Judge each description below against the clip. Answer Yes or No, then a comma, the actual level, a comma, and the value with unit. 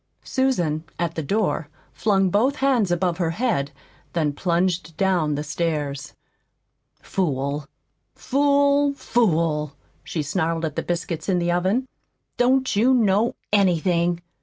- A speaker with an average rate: No, slow, 125 wpm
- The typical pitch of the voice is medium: Yes, medium, 175 Hz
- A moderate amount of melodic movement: No, wide, 5.7 semitones